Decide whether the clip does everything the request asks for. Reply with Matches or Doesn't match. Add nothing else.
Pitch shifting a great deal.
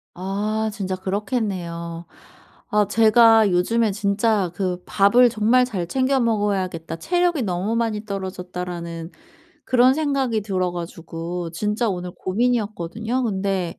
Doesn't match